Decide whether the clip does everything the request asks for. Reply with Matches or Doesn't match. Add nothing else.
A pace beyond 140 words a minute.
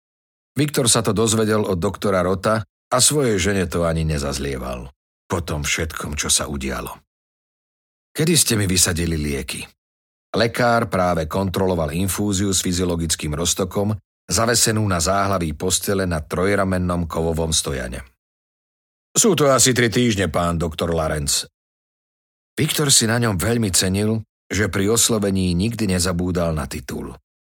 Doesn't match